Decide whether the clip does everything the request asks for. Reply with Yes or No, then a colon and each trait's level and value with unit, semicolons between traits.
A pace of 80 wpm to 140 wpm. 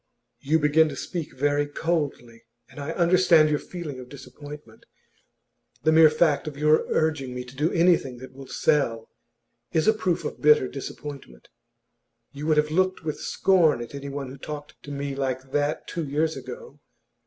No: average, 170 wpm